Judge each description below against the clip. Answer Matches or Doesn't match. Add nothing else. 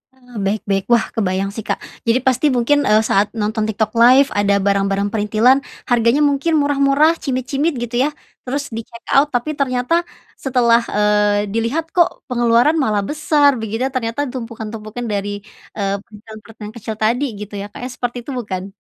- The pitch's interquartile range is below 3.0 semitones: Doesn't match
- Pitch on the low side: Doesn't match